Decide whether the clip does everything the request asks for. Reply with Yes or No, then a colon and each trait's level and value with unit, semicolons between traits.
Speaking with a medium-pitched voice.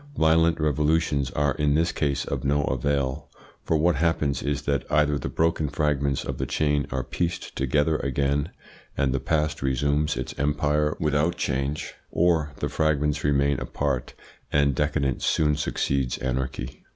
No: very low, 75 Hz